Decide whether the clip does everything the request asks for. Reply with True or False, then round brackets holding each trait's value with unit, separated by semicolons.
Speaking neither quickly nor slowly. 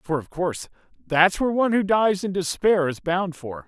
False (210 wpm)